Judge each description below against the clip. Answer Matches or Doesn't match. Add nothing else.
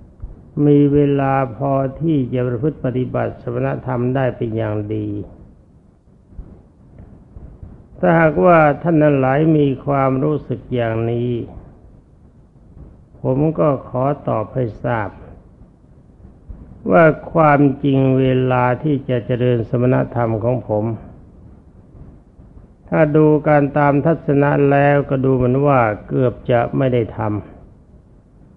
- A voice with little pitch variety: Doesn't match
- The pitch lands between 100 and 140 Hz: Matches